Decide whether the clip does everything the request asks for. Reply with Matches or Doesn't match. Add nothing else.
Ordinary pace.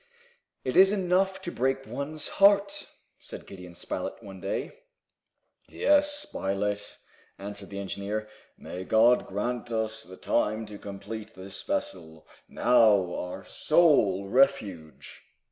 Doesn't match